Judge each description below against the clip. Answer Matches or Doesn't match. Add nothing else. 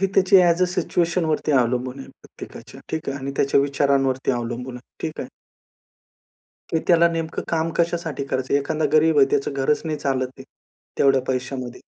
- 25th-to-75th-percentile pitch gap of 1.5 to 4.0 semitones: Matches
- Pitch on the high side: Doesn't match